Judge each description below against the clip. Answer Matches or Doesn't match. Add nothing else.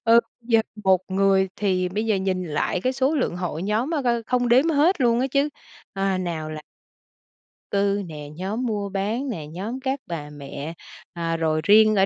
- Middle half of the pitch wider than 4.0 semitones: Matches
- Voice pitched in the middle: Doesn't match